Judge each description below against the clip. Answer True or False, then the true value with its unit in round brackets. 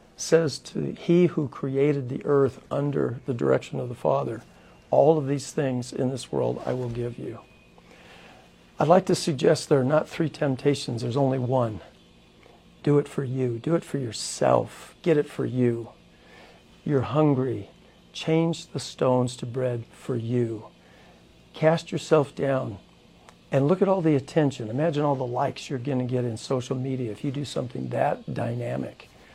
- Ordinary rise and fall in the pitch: True (3.4 semitones)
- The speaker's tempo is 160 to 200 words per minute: True (170 wpm)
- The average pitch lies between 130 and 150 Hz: True (135 Hz)